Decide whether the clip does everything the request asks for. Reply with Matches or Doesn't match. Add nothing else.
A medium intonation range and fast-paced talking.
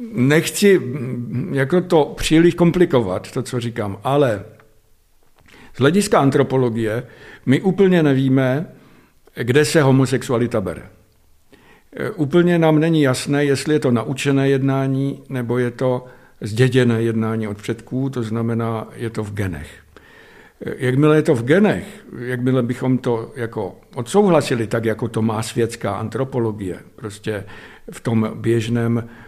Doesn't match